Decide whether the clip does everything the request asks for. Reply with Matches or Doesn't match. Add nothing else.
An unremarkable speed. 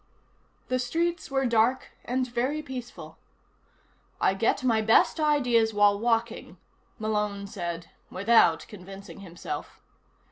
Doesn't match